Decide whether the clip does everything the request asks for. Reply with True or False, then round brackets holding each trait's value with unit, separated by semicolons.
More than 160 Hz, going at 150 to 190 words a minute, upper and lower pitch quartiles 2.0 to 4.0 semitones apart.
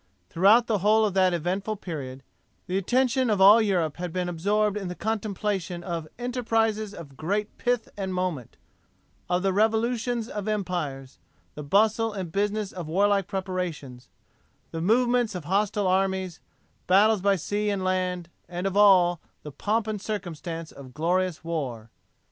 True (190 Hz; 155 wpm; 3.4 semitones)